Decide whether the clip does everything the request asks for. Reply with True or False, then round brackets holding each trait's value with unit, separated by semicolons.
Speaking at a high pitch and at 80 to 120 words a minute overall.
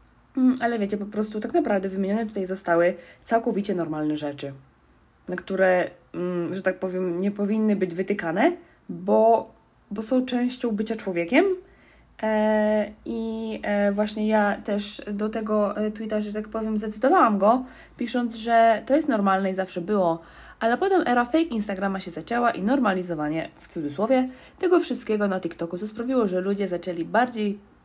False (210 Hz; 145 wpm)